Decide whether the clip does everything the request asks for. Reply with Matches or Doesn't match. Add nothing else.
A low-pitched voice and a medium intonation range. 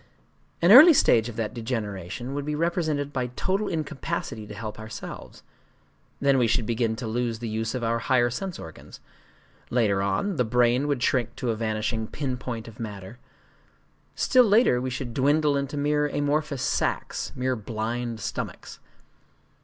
Matches